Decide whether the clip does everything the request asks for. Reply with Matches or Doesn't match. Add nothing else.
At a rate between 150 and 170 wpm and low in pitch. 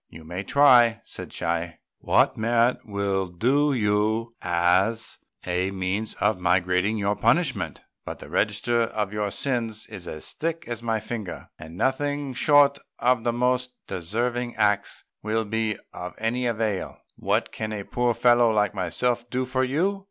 Matches